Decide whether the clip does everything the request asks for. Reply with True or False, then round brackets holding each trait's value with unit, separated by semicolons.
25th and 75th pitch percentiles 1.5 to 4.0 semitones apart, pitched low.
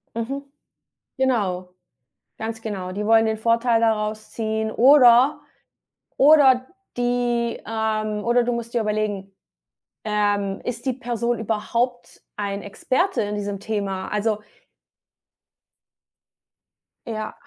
False (2.5 semitones; 225 Hz)